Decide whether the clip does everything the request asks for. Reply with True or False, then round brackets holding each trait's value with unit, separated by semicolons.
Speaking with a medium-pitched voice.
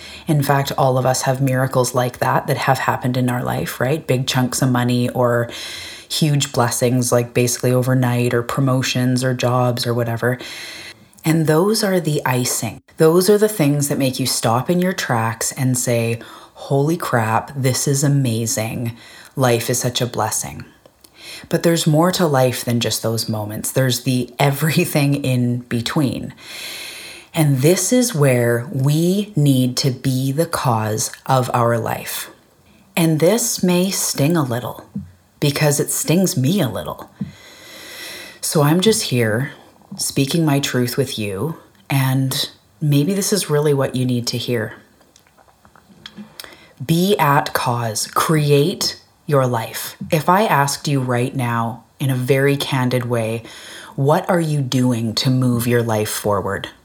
False (130 Hz)